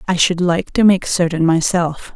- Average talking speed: Yes, average, 195 wpm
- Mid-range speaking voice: Yes, medium, 175 Hz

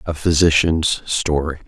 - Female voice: No, male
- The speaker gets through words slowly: Yes, slow, 105 wpm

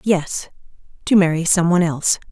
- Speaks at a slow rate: Yes, slow, 130 wpm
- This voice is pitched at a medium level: Yes, medium, 175 Hz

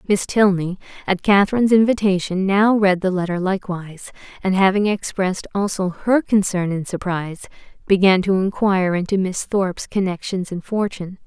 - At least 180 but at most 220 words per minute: No, average, 145 wpm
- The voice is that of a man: No, female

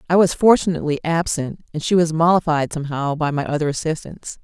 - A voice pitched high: No, medium, 160 Hz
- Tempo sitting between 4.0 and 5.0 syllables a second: No, 6.1 syllables/s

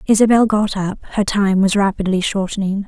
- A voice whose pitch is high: Yes, high, 200 Hz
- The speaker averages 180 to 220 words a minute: No, average, 165 wpm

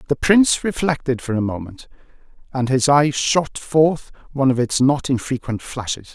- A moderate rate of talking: Yes, average, 165 wpm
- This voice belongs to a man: Yes, male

